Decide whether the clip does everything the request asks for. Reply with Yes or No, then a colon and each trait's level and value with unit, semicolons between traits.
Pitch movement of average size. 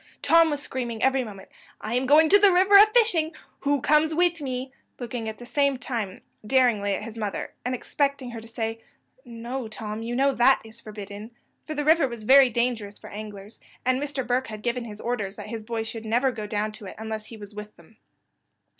Yes: average, 4.2 semitones